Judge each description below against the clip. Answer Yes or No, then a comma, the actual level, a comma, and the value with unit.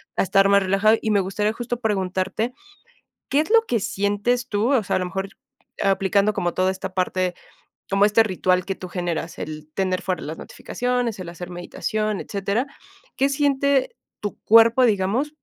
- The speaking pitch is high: Yes, high, 200 Hz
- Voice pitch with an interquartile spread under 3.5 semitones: No, average, 3.8 semitones